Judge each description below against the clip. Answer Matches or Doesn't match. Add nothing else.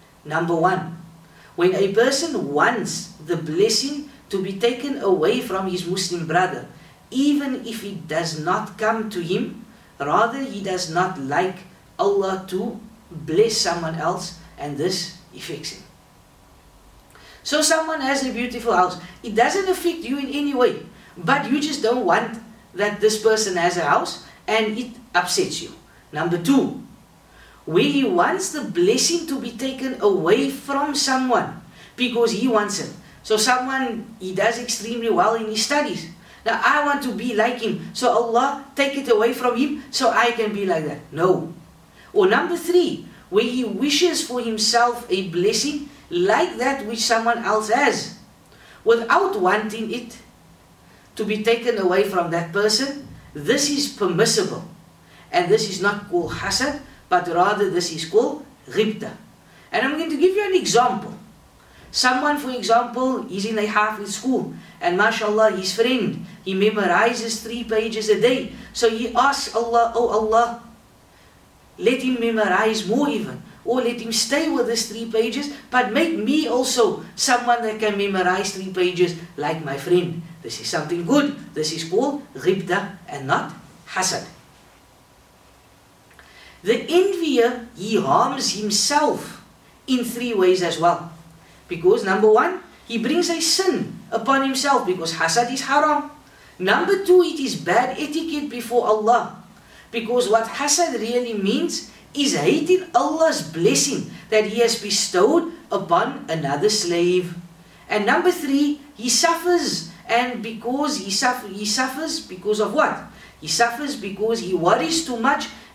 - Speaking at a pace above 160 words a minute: Doesn't match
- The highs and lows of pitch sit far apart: Matches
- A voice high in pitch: Matches